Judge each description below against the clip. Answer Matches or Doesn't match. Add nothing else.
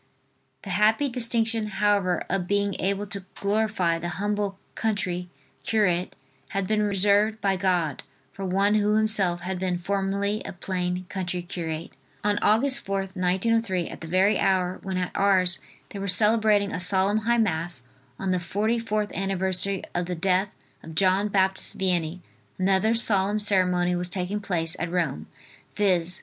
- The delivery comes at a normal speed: Matches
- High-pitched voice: Matches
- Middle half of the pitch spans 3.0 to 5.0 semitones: Doesn't match